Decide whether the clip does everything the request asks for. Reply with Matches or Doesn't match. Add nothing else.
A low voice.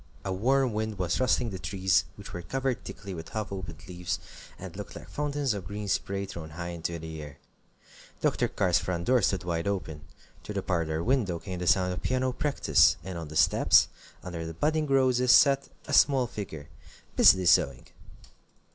Matches